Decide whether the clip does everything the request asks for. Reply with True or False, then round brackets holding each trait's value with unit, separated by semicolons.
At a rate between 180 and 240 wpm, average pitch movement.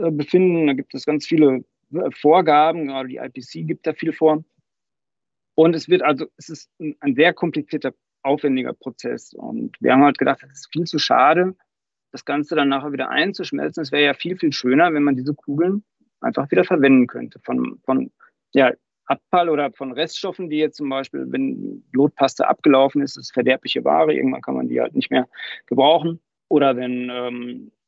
True (185 wpm; 3.3 semitones)